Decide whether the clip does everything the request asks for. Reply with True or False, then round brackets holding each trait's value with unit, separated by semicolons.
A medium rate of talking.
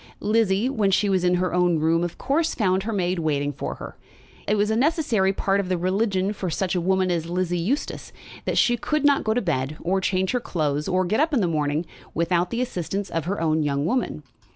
False (225 wpm)